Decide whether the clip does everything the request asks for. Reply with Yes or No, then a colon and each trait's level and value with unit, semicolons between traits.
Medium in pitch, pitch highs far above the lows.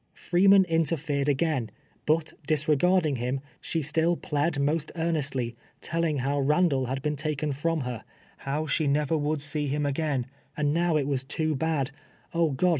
No: medium, 150 Hz; narrow, 2.6 semitones